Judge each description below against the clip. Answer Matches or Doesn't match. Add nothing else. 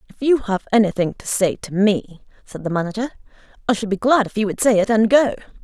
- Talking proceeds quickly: Matches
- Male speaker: Doesn't match